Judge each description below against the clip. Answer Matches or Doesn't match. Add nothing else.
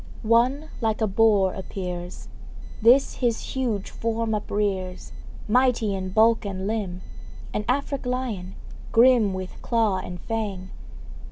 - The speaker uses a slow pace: Matches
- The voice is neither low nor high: Doesn't match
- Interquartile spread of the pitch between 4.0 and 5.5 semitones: Doesn't match